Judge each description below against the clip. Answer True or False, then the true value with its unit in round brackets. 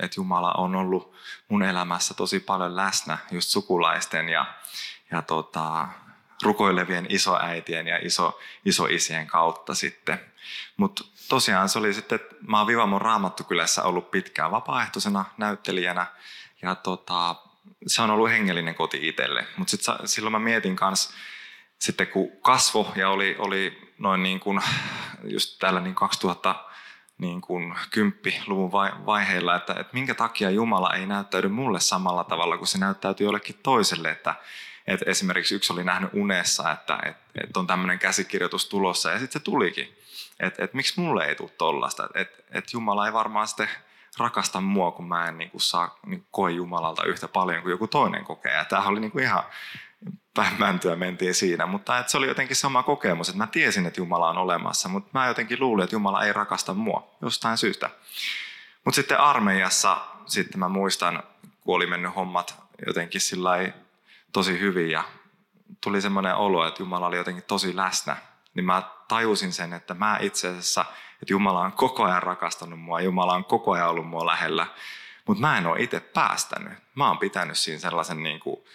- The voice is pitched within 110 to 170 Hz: False (95 Hz)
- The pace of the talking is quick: True (165 wpm)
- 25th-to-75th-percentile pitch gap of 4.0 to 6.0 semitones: False (3.2 semitones)